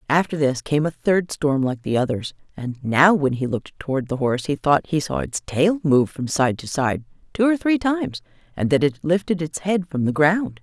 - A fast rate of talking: Yes, fast, 230 wpm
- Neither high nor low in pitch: Yes, medium, 150 Hz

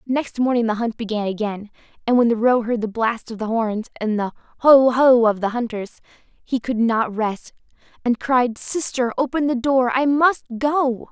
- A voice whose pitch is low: No, high, 240 Hz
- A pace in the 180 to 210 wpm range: Yes, average, 195 wpm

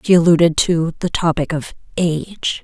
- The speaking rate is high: No, average, 160 wpm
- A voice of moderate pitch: Yes, medium, 165 Hz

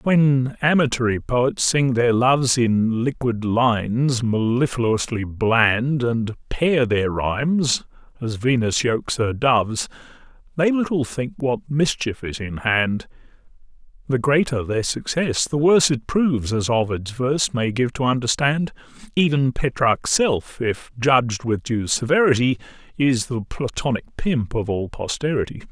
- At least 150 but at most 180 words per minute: No, slow, 135 wpm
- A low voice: Yes, low, 125 Hz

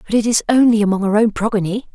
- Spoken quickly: Yes, fast, 245 wpm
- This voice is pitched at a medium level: No, high, 215 Hz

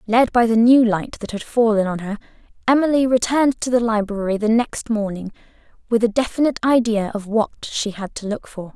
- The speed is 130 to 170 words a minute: No, average, 200 wpm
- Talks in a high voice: Yes, high, 225 Hz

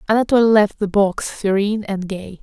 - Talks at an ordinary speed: Yes, average, 175 wpm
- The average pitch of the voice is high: Yes, high, 205 Hz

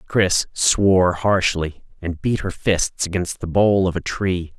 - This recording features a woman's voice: No, male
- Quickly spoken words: No, average, 170 wpm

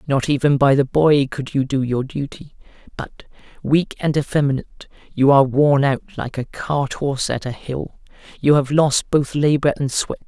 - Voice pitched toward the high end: No, medium, 140 Hz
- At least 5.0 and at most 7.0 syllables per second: No, 4.8 syllables/s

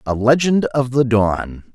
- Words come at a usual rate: Yes, average, 170 wpm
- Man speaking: Yes, male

